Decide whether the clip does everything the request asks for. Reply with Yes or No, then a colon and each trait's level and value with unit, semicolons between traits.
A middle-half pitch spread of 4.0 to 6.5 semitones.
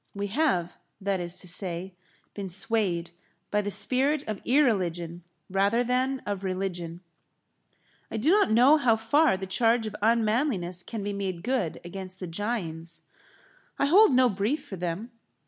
Yes: average, 5.1 semitones